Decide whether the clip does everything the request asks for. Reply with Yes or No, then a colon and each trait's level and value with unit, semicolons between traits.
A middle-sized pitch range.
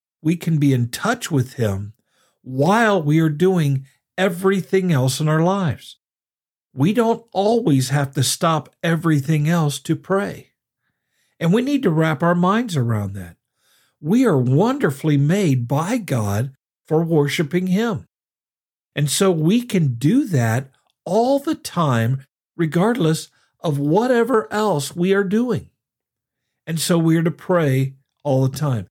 No: wide, 6.0 semitones